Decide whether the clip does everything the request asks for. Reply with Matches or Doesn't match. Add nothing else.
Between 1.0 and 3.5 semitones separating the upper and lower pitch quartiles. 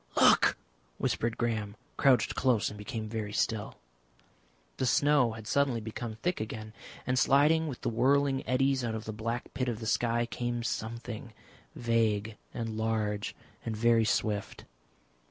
Matches